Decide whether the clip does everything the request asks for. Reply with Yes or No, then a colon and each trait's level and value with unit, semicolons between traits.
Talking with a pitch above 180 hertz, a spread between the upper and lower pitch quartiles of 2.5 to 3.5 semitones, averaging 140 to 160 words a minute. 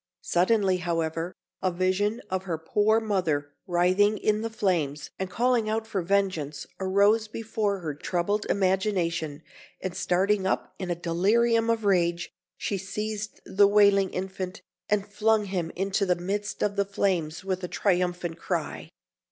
Yes: high, 190 Hz; average, 2.9 semitones; average, 150 wpm